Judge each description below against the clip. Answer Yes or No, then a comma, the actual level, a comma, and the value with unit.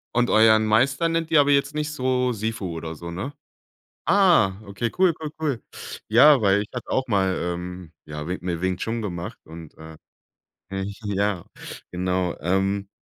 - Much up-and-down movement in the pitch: Yes, wide, 6.2 semitones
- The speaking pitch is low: Yes, low, 100 Hz